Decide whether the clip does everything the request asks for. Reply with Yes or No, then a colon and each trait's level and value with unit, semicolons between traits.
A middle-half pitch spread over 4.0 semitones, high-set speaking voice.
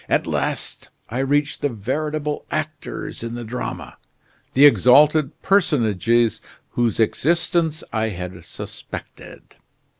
No: average, 5.0 semitones; low, 135 Hz